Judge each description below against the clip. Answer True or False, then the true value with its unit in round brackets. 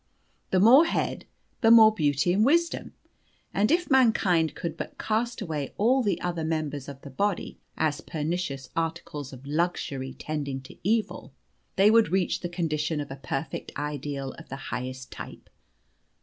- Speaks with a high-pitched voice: False (165 Hz)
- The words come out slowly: False (160 wpm)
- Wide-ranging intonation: True (6.6 semitones)